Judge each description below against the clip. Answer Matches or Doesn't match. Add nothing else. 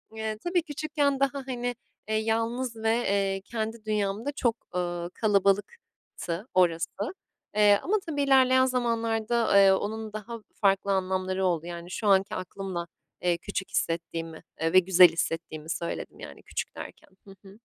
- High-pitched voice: Matches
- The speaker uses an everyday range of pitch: Matches